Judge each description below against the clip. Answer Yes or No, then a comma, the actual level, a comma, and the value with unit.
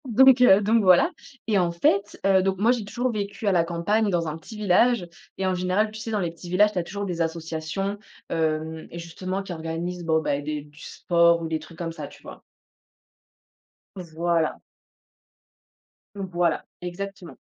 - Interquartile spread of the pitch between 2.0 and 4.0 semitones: Yes, average, 3.4 semitones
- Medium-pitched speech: Yes, medium, 180 Hz